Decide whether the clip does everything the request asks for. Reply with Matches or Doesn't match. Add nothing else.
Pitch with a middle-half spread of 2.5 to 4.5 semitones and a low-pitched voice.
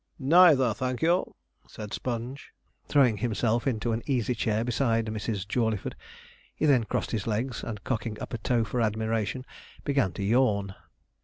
Matches